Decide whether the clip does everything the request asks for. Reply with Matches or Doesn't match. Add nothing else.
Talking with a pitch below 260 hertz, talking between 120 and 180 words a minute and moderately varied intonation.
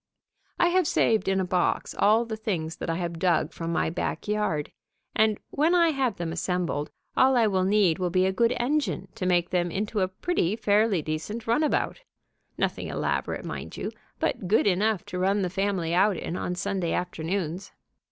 Doesn't match